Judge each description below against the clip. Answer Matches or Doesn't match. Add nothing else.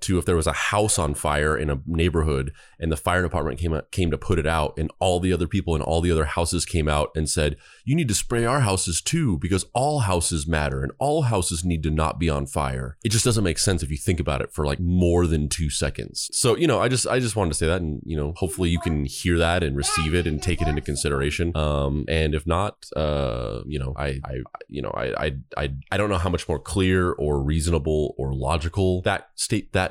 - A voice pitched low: Matches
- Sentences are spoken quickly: Matches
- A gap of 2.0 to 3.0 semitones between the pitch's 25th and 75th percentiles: Doesn't match